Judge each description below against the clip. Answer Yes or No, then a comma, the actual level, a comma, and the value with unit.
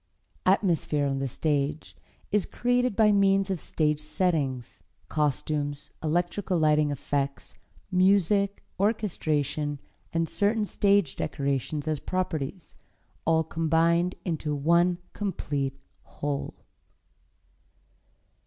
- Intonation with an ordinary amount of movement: Yes, average, 4.8 semitones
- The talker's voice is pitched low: No, medium, 160 Hz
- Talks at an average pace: No, slow, 95 wpm